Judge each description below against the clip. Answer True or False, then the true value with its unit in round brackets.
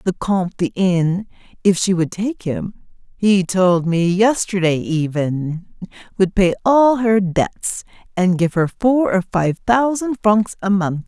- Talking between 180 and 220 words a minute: False (155 wpm)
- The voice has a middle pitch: False (195 Hz)